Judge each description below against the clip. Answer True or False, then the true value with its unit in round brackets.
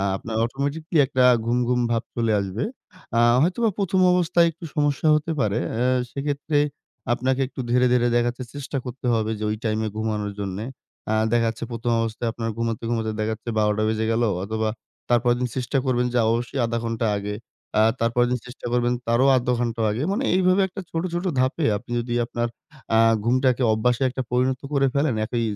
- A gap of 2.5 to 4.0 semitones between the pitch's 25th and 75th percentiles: True (3.1 semitones)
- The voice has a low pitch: True (120 Hz)